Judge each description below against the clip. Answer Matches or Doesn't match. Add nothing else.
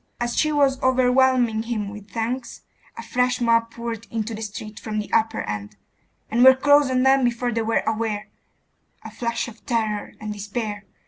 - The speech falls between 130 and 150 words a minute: Doesn't match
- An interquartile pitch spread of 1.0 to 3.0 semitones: Matches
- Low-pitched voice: Doesn't match